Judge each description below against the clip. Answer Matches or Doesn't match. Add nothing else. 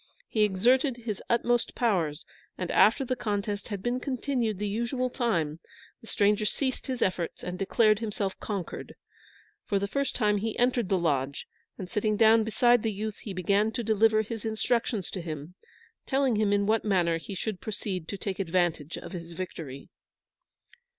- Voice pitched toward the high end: Matches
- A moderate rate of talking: Matches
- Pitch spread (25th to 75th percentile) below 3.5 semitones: Doesn't match